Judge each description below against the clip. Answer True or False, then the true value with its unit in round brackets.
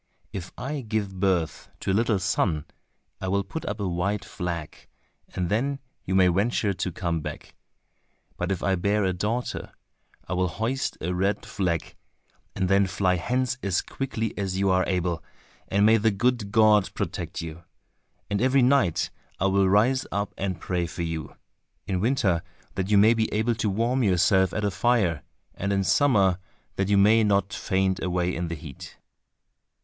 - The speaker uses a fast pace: False (175 wpm)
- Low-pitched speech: True (100 Hz)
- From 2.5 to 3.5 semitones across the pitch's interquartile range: True (3.2 semitones)